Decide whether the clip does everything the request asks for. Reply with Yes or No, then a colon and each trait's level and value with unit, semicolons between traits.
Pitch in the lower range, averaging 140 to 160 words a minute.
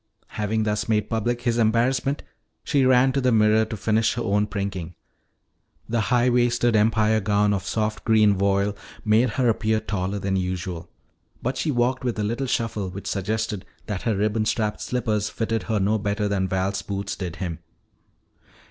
No: low, 110 Hz; average, 175 wpm